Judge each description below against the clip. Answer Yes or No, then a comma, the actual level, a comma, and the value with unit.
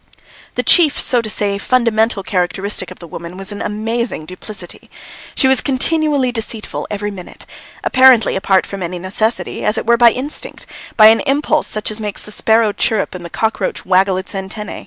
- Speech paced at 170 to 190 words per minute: Yes, average, 180 wpm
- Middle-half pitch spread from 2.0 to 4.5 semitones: Yes, average, 3.6 semitones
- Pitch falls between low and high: No, high, 215 Hz